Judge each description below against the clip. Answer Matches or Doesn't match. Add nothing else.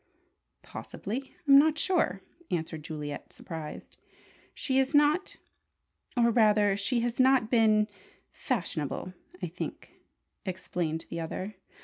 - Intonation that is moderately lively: Doesn't match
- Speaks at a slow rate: Matches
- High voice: Matches